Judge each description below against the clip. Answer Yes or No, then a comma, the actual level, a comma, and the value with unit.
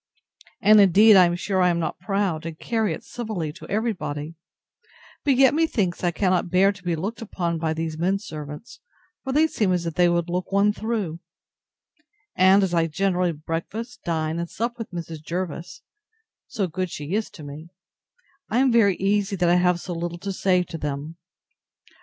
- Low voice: No, medium, 180 Hz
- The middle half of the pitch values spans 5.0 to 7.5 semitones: No, average, 3.6 semitones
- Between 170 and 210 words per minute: Yes, average, 190 wpm